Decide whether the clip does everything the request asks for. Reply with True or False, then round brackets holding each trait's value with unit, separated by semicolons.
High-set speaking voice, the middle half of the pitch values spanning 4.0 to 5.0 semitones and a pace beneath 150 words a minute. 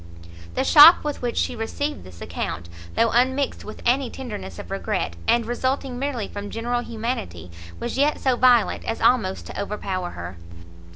False (235 Hz; 4.4 semitones; 165 wpm)